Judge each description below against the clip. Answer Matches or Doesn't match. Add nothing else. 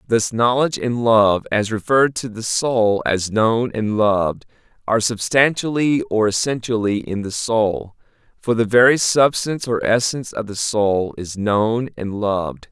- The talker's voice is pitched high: Doesn't match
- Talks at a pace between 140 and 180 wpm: Matches